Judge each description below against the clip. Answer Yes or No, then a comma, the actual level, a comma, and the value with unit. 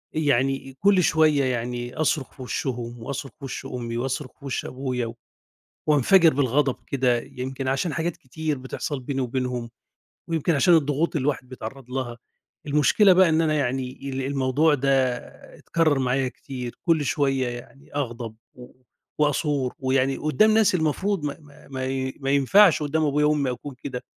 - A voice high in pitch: No, low, 135 Hz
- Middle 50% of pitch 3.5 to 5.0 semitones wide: No, average, 2.9 semitones